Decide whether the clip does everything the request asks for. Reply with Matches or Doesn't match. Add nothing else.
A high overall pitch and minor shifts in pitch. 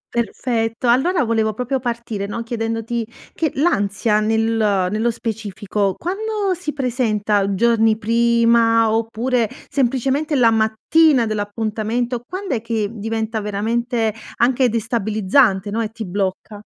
Matches